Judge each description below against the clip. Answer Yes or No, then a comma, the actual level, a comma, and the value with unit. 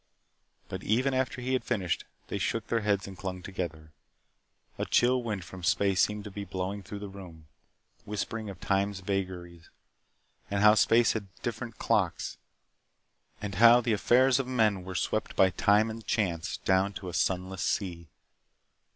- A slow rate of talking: No, average, 165 wpm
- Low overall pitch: Yes, low, 100 Hz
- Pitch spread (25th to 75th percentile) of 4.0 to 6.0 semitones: No, average, 3.3 semitones